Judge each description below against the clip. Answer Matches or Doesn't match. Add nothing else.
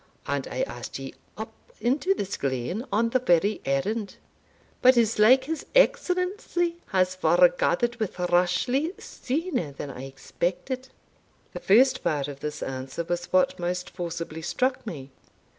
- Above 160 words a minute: Doesn't match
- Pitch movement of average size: Doesn't match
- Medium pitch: Doesn't match